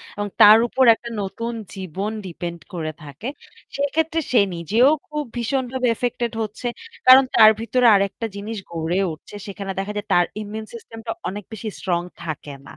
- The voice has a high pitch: Yes, high, 215 Hz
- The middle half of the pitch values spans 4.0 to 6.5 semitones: Yes, average, 4.3 semitones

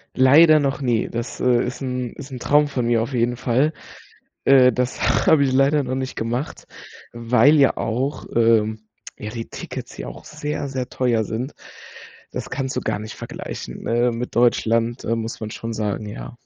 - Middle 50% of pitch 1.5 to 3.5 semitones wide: Yes, narrow, 2.6 semitones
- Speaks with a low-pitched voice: Yes, low, 125 Hz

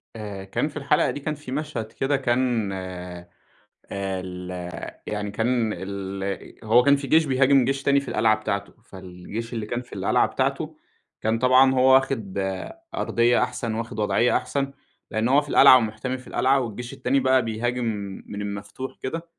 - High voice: No, low, 120 Hz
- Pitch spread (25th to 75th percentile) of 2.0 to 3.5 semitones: No, average, 4.4 semitones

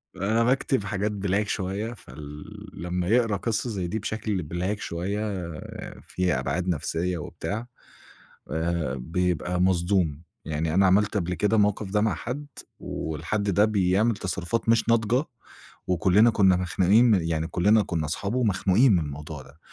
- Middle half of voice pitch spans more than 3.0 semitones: Yes, average, 3.6 semitones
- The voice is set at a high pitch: No, very low, 95 Hz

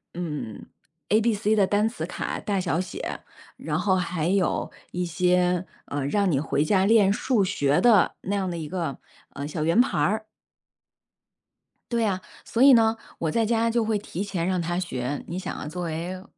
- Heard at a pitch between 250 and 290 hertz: No, medium, 185 Hz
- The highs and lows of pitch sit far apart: No, average, 4.0 semitones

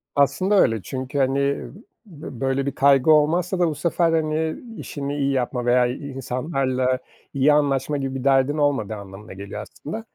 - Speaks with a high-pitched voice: No, medium, 140 Hz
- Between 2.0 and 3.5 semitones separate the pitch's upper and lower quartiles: Yes, average, 2.9 semitones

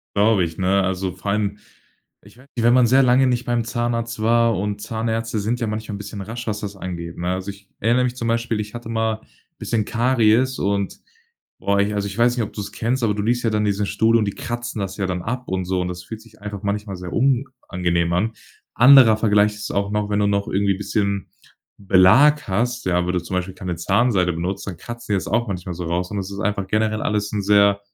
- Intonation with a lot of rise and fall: No, average, 3.2 semitones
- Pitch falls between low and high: No, low, 105 Hz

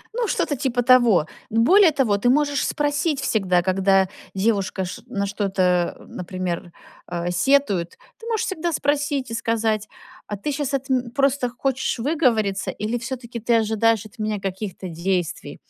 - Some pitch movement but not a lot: No, wide, 5.9 semitones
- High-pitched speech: Yes, high, 230 Hz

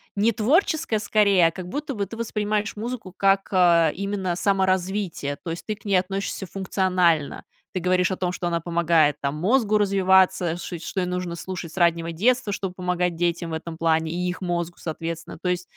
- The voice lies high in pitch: No, medium, 180 Hz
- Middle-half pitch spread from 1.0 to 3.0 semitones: Yes, average, 2.7 semitones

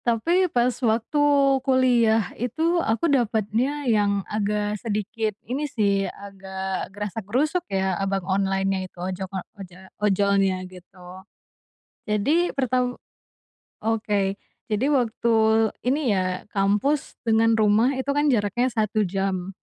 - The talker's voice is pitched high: Yes, high, 210 Hz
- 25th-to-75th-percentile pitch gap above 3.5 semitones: Yes, average, 4.2 semitones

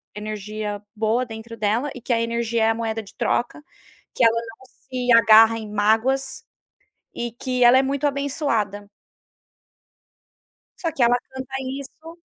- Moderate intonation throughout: Yes, average, 3.0 semitones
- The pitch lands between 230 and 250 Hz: Yes, high, 235 Hz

